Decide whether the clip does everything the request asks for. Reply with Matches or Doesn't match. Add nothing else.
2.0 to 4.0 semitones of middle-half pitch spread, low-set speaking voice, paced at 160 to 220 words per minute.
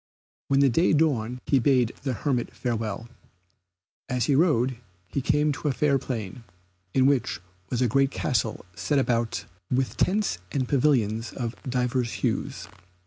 Doesn't match